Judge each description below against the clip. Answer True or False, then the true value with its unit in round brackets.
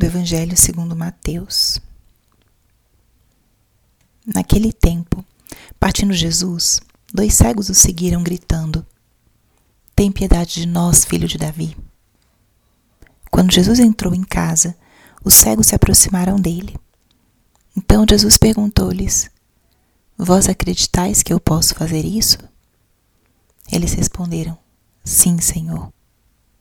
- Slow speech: True (100 wpm)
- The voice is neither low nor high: True (165 Hz)